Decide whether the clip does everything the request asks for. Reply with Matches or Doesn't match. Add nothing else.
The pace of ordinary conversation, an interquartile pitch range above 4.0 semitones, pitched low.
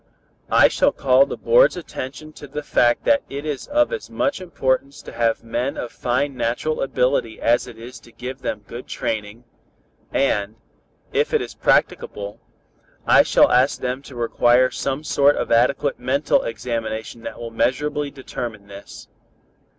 Doesn't match